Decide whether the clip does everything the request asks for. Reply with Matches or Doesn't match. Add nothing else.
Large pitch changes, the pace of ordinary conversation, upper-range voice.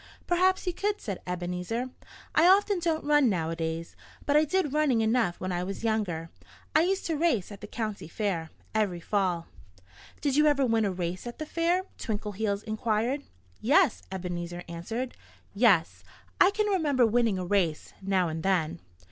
Matches